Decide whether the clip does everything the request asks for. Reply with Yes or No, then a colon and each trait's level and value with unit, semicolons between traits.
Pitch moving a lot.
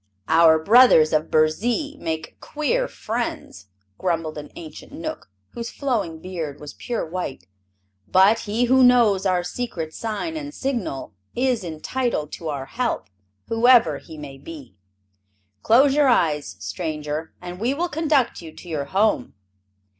Yes: wide, 7.9 semitones